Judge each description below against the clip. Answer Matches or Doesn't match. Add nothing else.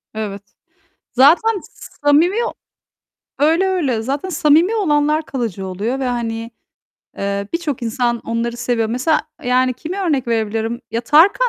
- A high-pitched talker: Matches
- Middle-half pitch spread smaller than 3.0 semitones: Doesn't match